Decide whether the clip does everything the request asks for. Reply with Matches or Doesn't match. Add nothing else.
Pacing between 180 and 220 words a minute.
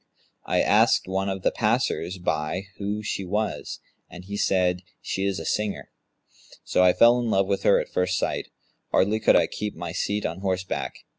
Matches